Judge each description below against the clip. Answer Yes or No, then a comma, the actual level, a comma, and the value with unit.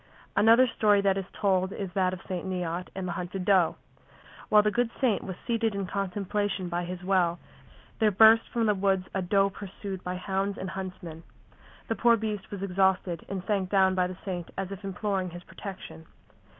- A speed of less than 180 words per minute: No, average, 190 wpm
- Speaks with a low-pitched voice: No, high, 190 Hz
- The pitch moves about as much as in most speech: No, narrow, 2.0 semitones